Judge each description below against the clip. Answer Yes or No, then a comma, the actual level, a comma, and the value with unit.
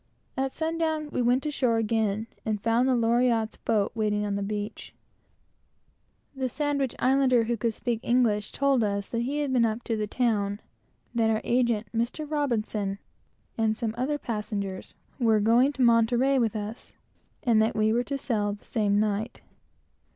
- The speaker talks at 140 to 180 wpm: Yes, average, 170 wpm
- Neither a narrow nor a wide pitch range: Yes, average, 3.0 semitones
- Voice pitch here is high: Yes, high, 230 Hz